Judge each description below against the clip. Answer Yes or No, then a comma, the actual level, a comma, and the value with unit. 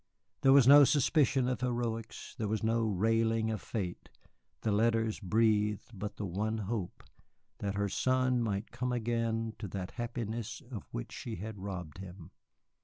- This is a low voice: Yes, low, 110 Hz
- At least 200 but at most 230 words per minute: No, average, 160 wpm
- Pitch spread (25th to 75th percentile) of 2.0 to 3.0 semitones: Yes, average, 2.7 semitones